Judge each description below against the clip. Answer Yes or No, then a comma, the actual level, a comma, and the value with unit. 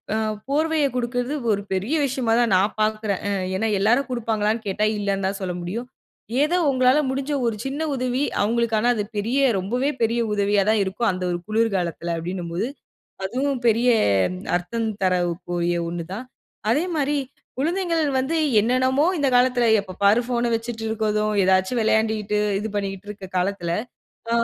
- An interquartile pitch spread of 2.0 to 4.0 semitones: No, average, 4.4 semitones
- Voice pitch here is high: Yes, high, 220 Hz